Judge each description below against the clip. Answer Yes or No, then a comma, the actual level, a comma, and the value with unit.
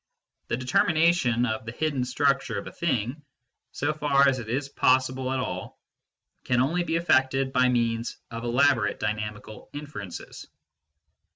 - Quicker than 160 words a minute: No, average, 145 wpm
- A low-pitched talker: Yes, low, 130 Hz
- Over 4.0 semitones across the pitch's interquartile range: No, average, 3.6 semitones